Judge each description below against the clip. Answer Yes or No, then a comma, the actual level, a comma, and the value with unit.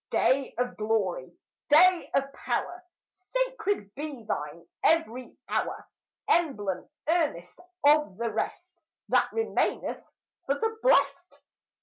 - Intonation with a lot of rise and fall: Yes, wide, 8.2 semitones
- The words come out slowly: Yes, slow, 105 wpm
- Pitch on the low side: No, very high, 295 Hz